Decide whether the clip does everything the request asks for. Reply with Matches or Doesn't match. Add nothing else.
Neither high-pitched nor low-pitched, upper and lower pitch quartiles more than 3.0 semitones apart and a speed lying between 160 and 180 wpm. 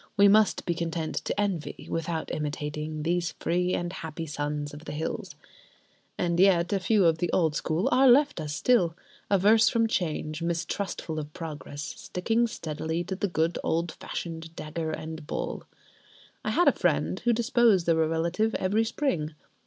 Matches